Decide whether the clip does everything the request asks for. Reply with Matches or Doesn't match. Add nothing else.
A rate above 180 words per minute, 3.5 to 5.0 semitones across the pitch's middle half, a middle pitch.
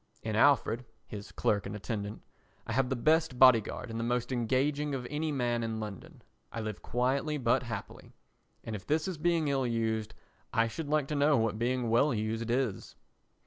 Doesn't match